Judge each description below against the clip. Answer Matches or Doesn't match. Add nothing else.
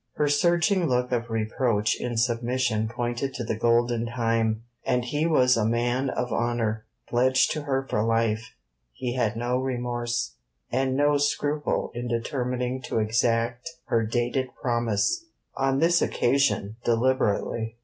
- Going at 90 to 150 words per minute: Matches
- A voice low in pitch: Matches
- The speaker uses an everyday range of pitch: Doesn't match